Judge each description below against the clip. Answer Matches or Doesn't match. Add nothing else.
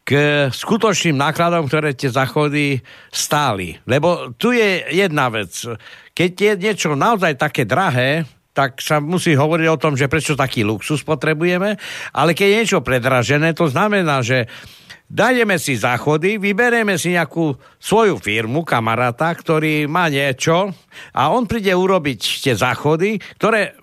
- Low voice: Doesn't match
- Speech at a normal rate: Matches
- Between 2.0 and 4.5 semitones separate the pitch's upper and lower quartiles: Doesn't match